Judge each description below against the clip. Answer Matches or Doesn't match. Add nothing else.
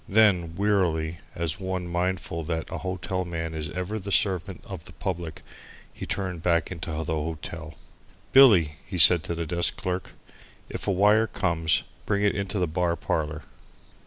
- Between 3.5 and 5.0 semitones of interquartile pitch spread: Doesn't match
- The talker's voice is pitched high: Doesn't match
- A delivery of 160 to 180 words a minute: Matches